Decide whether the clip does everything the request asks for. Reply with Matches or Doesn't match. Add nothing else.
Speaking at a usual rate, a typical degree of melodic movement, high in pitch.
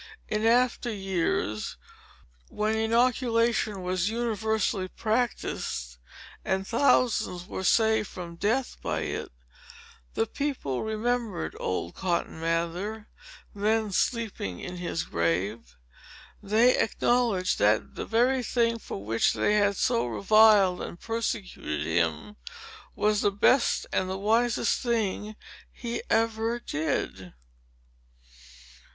Doesn't match